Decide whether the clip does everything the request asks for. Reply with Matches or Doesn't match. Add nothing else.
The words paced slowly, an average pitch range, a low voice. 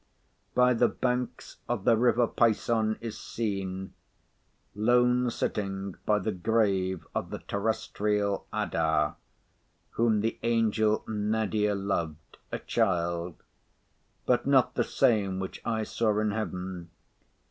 Matches